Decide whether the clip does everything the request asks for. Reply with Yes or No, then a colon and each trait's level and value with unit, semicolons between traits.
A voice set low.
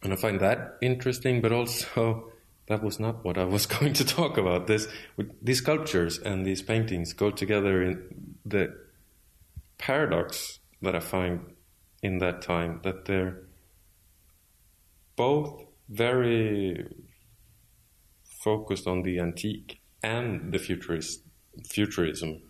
Yes: very low, 95 Hz